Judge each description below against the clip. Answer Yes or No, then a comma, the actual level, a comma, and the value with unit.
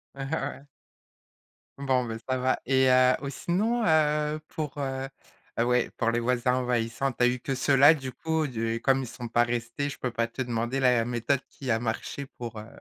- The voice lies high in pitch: No, low, 130 Hz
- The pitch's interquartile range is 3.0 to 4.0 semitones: No, narrow, 2.6 semitones